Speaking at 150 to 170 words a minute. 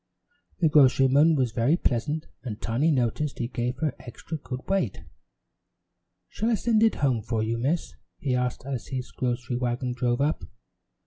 Yes: average, 165 wpm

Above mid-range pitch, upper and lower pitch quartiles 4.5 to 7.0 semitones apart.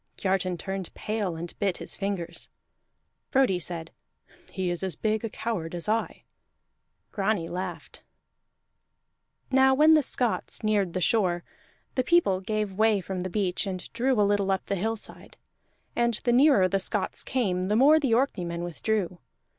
No: high, 200 Hz; average, 3.8 semitones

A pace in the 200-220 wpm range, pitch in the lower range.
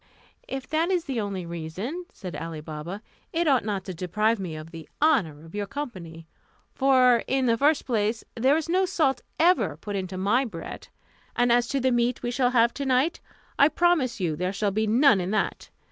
No: fast, 205 wpm; high, 230 Hz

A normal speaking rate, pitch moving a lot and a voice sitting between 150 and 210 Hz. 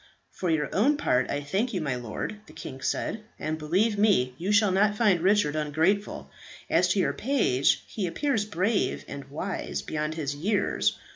Yes: average, 180 wpm; wide, 5.9 semitones; medium, 185 Hz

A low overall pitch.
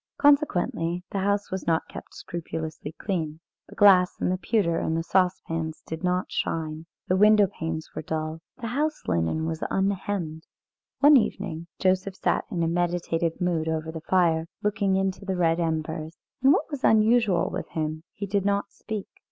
No: medium, 180 Hz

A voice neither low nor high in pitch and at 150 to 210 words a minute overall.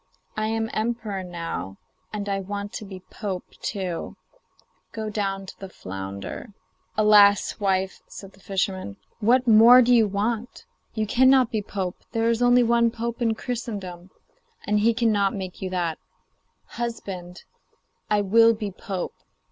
No: high, 205 Hz; average, 155 wpm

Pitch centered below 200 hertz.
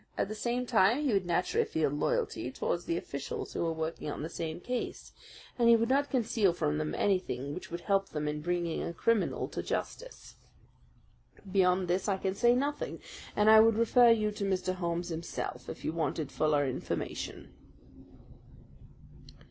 Yes: medium, 185 Hz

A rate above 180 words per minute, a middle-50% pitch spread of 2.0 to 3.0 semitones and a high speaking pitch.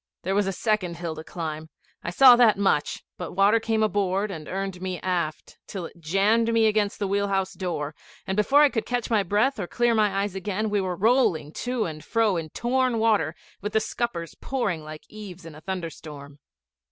No: fast, 205 wpm; average, 4.3 semitones; high, 195 Hz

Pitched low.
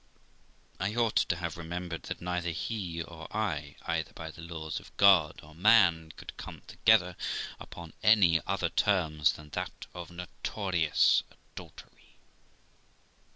Yes: very low, 85 Hz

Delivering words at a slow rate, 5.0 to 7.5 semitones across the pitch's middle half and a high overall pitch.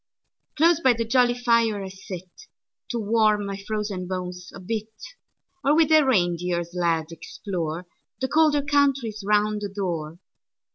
Yes: slow, 130 wpm; wide, 5.4 semitones; high, 210 Hz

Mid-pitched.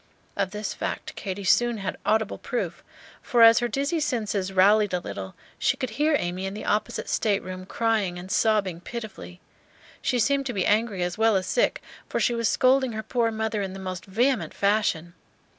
No: high, 215 Hz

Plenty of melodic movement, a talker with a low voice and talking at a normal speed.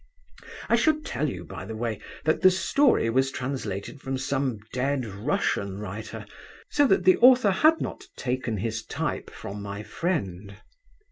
Yes: wide, 8.8 semitones; low, 130 Hz; average, 155 wpm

